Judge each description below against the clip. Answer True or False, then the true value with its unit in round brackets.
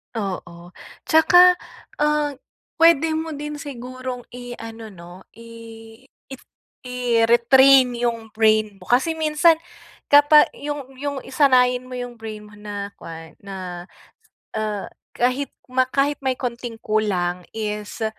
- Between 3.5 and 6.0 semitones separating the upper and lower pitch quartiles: True (4.6 semitones)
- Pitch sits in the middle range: False (245 Hz)